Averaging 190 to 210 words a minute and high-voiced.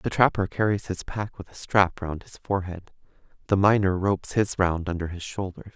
No: average, 200 wpm; very low, 95 Hz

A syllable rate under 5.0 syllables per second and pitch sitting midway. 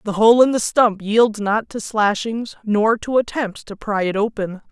No: 4.3 syllables/s; high, 215 Hz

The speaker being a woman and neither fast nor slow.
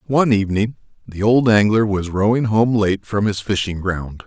No: male; average, 185 wpm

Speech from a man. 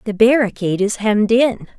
No: female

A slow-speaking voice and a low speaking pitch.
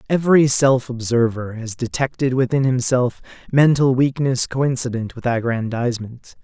Yes: slow, 110 wpm; low, 125 Hz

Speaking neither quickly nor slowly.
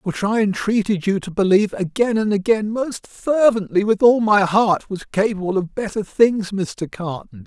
Yes: average, 175 wpm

